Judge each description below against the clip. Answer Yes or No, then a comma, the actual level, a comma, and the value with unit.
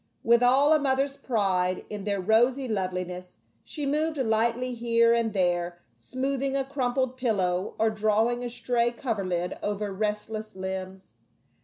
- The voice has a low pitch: No, high, 225 Hz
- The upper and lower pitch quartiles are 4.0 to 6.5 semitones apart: Yes, average, 4.8 semitones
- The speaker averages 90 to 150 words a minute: Yes, average, 140 wpm